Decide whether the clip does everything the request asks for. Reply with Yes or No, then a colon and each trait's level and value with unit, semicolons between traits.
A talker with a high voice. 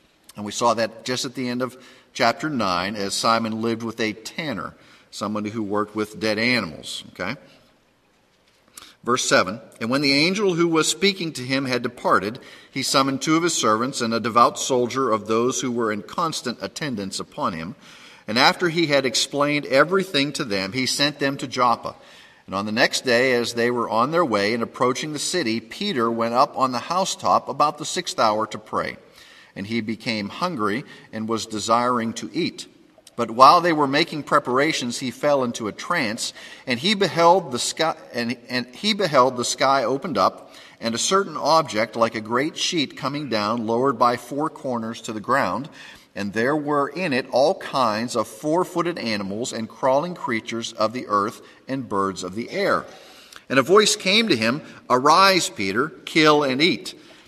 No: low, 125 Hz